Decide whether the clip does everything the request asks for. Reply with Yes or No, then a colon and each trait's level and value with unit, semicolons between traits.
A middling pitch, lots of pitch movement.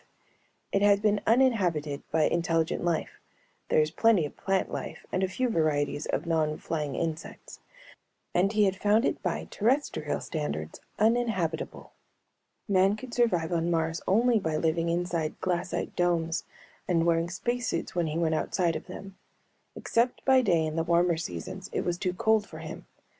No: medium, 175 Hz; average, 4.1 semitones